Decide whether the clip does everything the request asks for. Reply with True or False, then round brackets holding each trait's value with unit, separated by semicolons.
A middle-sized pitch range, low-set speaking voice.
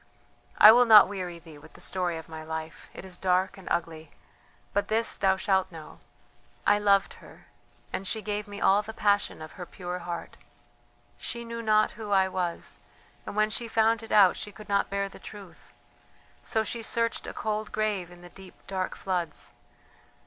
False (3.2 semitones; 195 Hz)